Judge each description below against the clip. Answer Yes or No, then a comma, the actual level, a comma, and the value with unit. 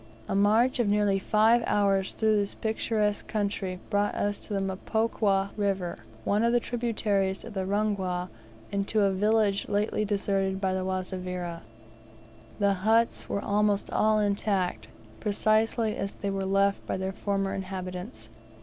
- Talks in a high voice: Yes, high, 200 Hz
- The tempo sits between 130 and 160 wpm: Yes, average, 150 wpm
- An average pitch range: No, narrow, 1.8 semitones